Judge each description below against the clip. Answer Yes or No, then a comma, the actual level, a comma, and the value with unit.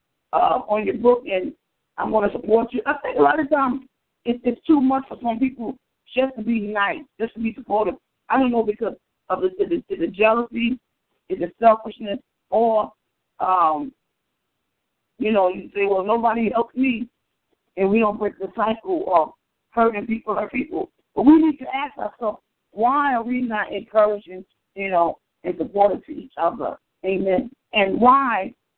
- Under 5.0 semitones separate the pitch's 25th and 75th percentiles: Yes, average, 4.2 semitones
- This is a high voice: Yes, high, 230 Hz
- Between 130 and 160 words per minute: No, average, 175 wpm